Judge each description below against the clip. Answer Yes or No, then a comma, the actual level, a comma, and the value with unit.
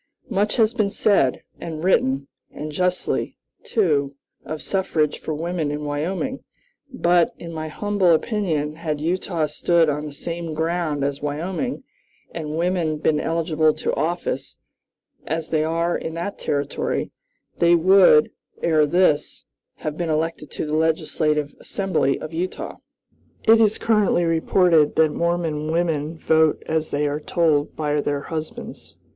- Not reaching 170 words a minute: Yes, average, 140 wpm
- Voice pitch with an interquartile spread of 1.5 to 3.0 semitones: Yes, narrow, 2.5 semitones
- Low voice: No, medium, 160 Hz